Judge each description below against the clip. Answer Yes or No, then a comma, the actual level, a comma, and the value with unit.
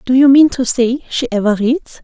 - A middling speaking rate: No, fast, 235 wpm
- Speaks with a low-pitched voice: No, very high, 250 Hz